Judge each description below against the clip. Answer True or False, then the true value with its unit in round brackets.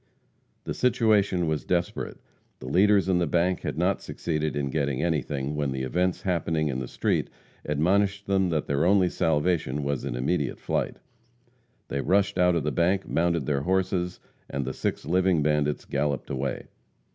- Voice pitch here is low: True (85 Hz)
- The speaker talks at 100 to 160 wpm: False (170 wpm)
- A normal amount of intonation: True (4.3 semitones)